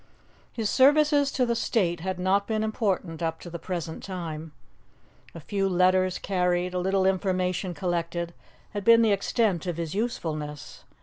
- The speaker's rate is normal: Yes, average, 160 wpm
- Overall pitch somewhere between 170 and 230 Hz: Yes, medium, 185 Hz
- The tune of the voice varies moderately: Yes, average, 3.3 semitones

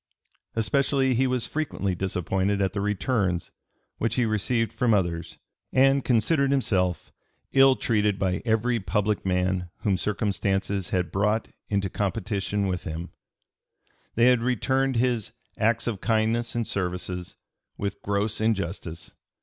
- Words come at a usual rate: No, slow, 130 wpm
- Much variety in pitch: No, average, 3.8 semitones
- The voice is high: No, low, 105 Hz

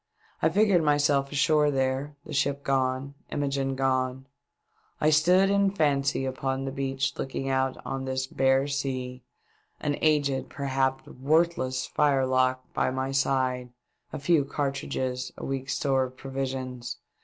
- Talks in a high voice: No, low, 135 Hz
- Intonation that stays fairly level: Yes, narrow, 1.5 semitones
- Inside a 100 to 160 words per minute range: Yes, average, 145 wpm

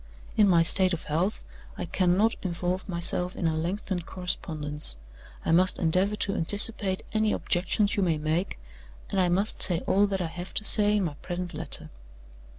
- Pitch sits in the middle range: Yes, medium, 180 Hz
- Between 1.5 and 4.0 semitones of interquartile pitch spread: Yes, average, 2.8 semitones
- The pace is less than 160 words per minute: No, average, 175 wpm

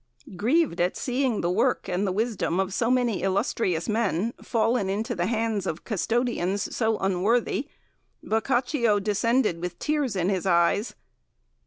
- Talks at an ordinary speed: Yes, average, 145 wpm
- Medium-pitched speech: No, high, 215 Hz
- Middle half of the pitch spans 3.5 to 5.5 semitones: Yes, average, 4.2 semitones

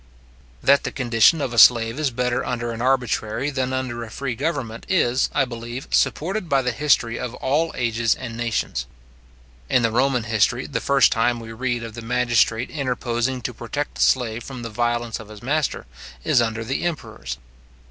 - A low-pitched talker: Yes, low, 120 Hz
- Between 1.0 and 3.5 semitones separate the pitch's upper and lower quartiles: Yes, narrow, 2.5 semitones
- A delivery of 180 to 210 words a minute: Yes, average, 185 wpm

